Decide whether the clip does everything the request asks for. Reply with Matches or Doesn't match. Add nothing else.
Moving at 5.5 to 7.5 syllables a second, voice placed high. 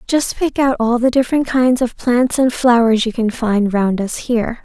Doesn't match